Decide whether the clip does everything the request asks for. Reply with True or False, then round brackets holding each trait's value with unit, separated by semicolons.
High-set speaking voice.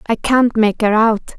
True (220 Hz)